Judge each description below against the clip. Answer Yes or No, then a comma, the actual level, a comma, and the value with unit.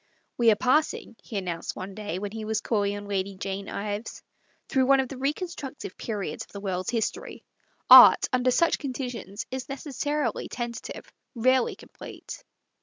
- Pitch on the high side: Yes, high, 225 Hz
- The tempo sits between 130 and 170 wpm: No, average, 180 wpm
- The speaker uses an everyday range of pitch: Yes, average, 4.4 semitones